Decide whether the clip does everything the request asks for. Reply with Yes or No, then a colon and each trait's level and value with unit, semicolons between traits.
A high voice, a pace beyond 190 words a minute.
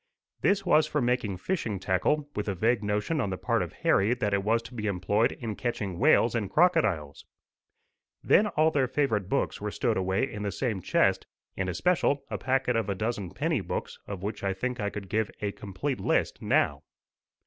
No: low, 110 Hz; average, 200 wpm